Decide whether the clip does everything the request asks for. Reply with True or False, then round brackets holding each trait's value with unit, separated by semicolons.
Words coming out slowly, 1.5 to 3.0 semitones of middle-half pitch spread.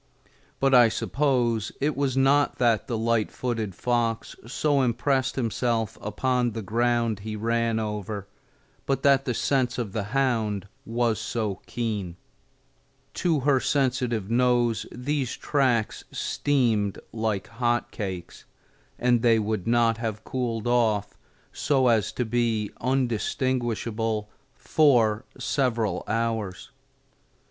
True (120 wpm; 2.7 semitones)